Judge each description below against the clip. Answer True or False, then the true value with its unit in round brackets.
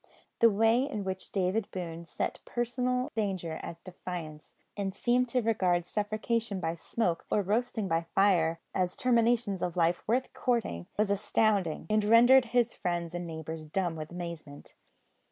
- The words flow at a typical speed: True (155 wpm)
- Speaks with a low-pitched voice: False (195 Hz)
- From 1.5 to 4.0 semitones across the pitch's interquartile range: False (5.2 semitones)